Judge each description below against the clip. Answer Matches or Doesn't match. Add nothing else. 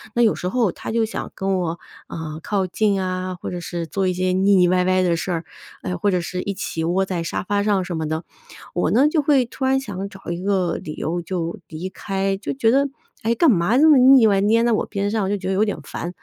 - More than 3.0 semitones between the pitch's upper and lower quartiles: Matches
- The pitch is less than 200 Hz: Matches